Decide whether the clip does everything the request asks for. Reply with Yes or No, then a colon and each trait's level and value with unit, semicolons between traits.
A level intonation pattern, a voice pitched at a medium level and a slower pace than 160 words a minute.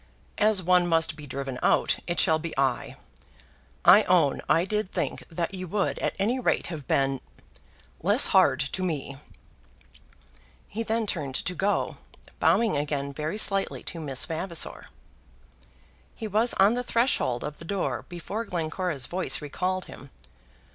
No: average, 5.0 semitones; medium, 175 Hz; average, 150 wpm